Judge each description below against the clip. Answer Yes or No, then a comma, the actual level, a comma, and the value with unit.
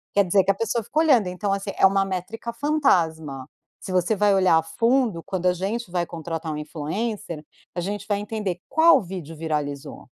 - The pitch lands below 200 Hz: Yes, high, 190 Hz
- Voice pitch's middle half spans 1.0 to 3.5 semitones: No, average, 4.4 semitones